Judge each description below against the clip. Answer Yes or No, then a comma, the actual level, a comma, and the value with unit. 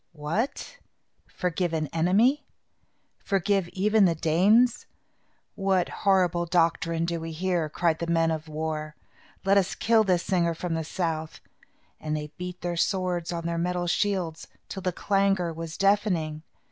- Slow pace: No, average, 145 wpm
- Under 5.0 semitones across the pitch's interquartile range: Yes, average, 2.9 semitones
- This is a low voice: No, medium, 175 Hz